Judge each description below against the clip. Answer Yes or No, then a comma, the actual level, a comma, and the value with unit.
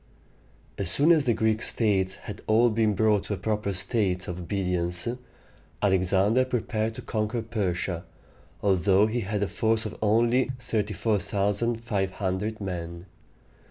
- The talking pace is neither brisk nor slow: No, slow, 130 wpm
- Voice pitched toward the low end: Yes, low, 105 Hz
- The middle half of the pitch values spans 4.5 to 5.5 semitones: No, average, 2.9 semitones